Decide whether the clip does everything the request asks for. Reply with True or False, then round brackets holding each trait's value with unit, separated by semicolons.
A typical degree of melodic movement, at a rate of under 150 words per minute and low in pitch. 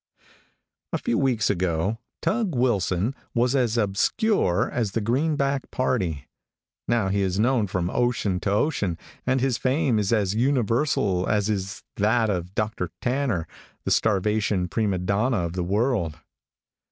True (4.7 semitones; 140 wpm; 105 Hz)